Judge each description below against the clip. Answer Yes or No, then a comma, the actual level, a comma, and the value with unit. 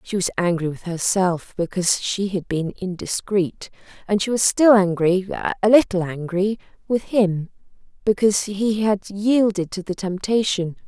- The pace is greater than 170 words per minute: No, average, 140 wpm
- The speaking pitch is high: Yes, high, 195 Hz